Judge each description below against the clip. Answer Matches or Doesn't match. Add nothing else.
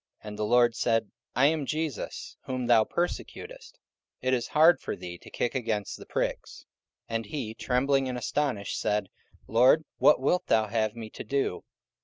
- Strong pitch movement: Doesn't match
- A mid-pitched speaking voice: Doesn't match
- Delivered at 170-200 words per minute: Matches